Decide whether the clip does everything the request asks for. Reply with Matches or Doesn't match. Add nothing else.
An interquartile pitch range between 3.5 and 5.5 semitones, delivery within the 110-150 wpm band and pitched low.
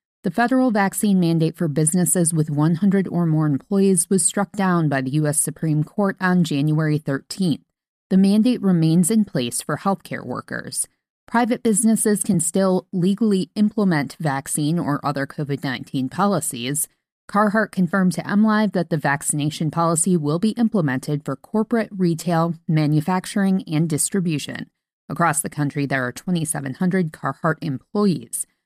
Doesn't match